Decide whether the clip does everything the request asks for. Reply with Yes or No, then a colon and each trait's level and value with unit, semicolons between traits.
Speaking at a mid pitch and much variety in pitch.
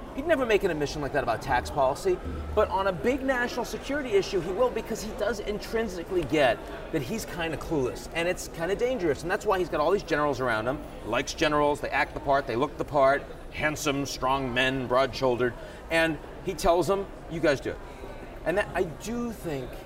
Yes: medium, 175 Hz; wide, 7.5 semitones